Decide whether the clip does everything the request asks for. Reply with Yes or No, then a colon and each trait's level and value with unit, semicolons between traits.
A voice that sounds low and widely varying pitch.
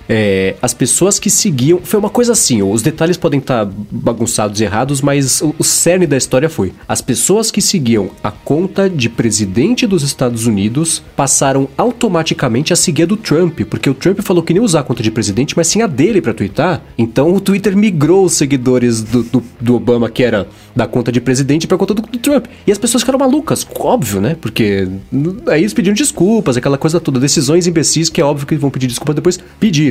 No: medium, 150 Hz; wide, 7.0 semitones